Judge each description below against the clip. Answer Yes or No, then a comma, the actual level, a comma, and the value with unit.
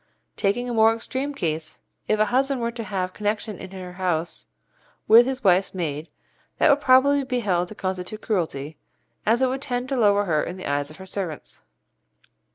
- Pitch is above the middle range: Yes, high, 205 Hz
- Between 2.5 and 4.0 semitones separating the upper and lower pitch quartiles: No, wide, 5.5 semitones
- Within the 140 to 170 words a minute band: No, average, 190 wpm